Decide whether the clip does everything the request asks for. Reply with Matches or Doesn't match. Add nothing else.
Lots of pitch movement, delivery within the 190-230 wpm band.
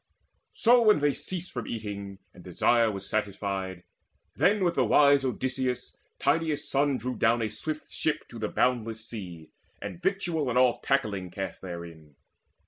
Doesn't match